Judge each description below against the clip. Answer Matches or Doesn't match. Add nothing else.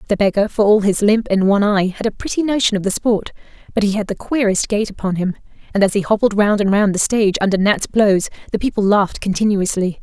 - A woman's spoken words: Matches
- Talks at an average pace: Doesn't match